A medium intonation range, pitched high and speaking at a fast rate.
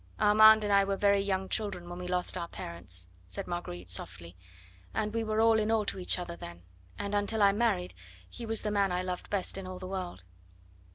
Yes: average, 3.1 semitones; high, 195 Hz; fast, 220 wpm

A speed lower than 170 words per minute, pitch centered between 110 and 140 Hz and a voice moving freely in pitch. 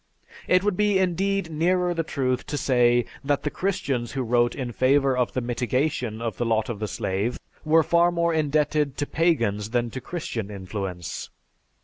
No: average, 175 wpm; low, 135 Hz; wide, 5.7 semitones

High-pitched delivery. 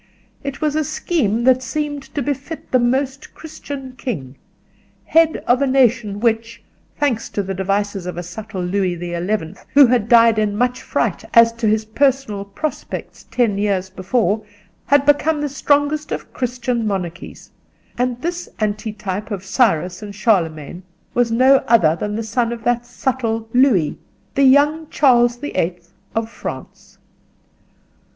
Yes: high, 230 Hz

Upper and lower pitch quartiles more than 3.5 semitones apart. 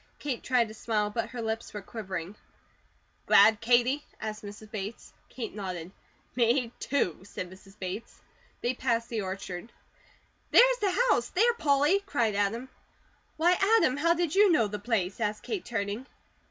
Yes: average, 5.0 semitones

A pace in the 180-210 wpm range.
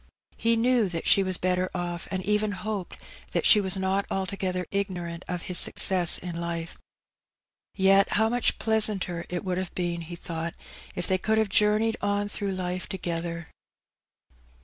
No: average, 165 wpm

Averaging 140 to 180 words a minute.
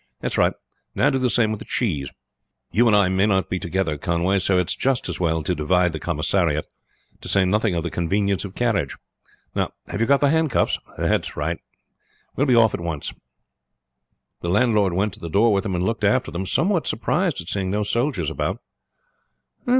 No: fast, 205 wpm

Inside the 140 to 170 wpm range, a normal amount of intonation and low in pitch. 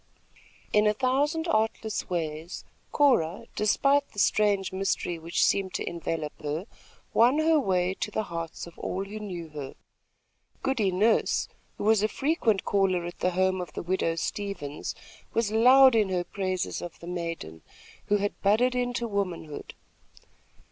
No: average, 155 wpm; average, 4.4 semitones; high, 195 Hz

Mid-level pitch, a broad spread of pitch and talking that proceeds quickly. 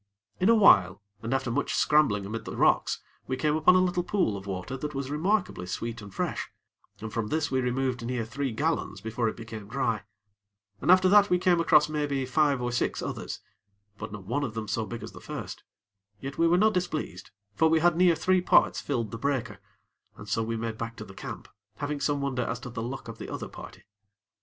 No: low, 130 Hz; wide, 5.8 semitones; fast, 225 wpm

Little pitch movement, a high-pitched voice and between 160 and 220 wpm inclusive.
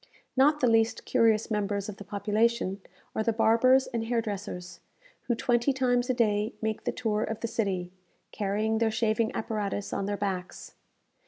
Yes: narrow, 2.3 semitones; high, 220 Hz; average, 170 wpm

